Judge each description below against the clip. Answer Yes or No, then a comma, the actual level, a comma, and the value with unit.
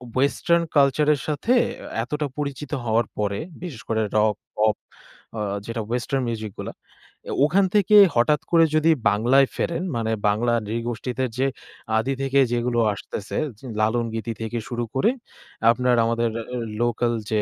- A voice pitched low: Yes, low, 120 Hz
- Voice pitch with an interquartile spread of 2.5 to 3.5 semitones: No, average, 4.0 semitones